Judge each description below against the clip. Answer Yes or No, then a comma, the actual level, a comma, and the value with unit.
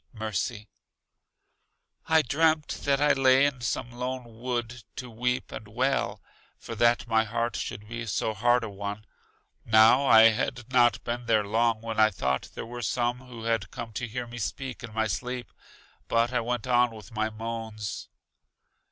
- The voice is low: Yes, low, 120 Hz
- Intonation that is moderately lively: No, narrow, 2.0 semitones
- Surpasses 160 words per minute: Yes, average, 170 wpm